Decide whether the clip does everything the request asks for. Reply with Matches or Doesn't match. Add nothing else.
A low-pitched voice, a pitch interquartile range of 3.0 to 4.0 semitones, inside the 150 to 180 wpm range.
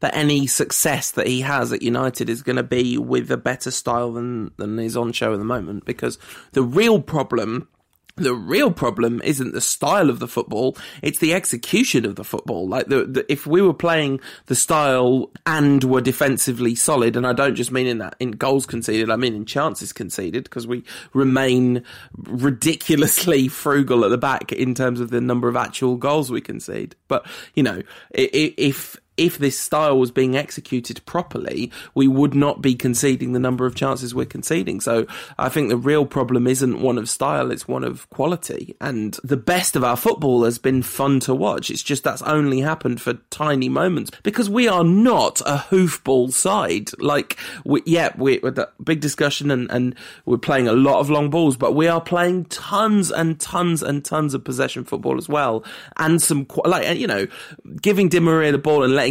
Doesn't match